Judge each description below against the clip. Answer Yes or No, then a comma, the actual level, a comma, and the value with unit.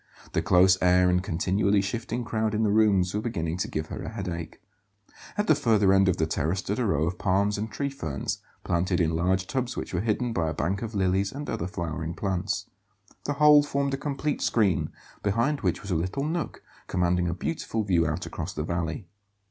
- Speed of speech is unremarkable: No, fast, 210 wpm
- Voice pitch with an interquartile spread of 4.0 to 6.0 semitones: Yes, average, 4.4 semitones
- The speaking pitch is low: Yes, very low, 95 Hz